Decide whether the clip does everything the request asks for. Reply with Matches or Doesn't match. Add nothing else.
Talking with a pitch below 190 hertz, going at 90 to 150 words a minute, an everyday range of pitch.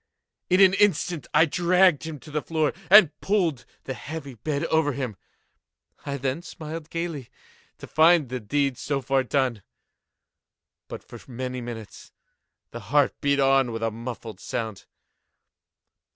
Matches